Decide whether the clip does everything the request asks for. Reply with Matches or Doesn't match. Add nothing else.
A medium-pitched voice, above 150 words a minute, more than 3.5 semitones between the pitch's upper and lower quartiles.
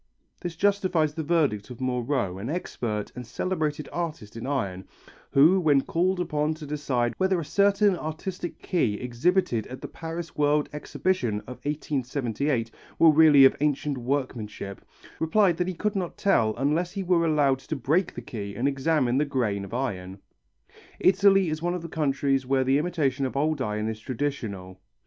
Matches